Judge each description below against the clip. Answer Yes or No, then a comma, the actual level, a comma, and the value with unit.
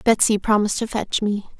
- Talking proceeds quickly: No, average, 190 wpm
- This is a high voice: Yes, high, 210 Hz